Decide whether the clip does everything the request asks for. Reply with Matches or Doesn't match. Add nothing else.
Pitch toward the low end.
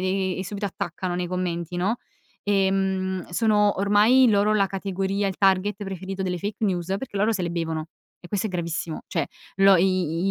Doesn't match